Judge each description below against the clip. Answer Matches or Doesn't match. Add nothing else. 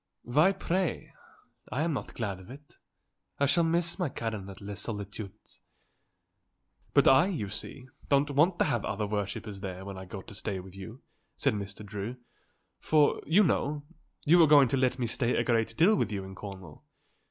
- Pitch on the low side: Matches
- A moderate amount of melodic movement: Doesn't match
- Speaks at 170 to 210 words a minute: Matches